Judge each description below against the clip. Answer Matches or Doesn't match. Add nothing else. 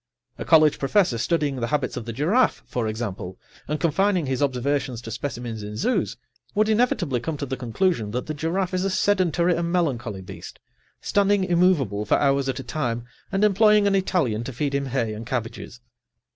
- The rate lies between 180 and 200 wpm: Matches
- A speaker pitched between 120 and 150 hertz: Matches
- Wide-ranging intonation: Matches